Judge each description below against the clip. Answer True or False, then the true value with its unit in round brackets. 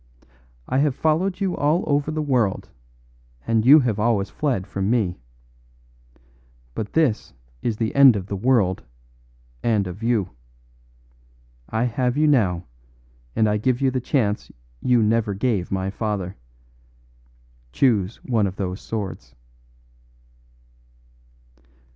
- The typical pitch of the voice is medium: False (115 Hz)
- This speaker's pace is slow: True (125 wpm)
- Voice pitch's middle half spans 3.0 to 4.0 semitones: False (4.7 semitones)